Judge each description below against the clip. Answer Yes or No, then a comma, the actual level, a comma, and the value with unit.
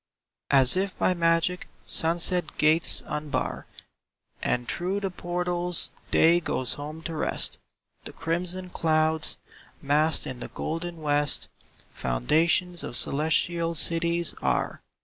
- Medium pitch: Yes, medium, 165 Hz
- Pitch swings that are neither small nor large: No, narrow, 2.3 semitones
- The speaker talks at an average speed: No, slow, 115 wpm